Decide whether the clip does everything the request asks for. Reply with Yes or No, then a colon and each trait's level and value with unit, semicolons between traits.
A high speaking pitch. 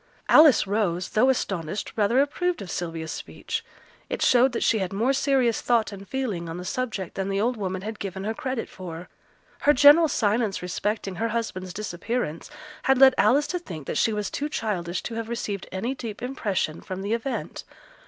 Yes: high, 215 Hz